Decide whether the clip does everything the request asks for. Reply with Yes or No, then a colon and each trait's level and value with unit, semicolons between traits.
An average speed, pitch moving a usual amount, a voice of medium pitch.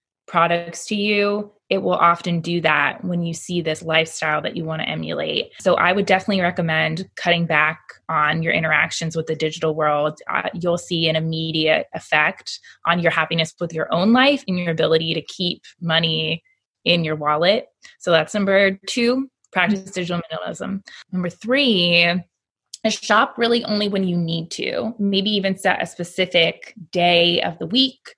Yes: average, 170 wpm; average, 3.5 semitones; medium, 175 Hz